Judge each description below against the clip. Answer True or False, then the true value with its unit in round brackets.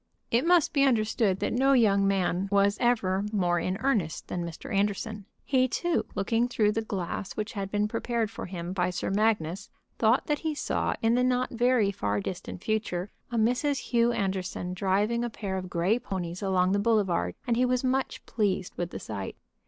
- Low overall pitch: False (210 Hz)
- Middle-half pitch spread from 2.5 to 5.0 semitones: True (4.2 semitones)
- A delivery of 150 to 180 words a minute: False (190 wpm)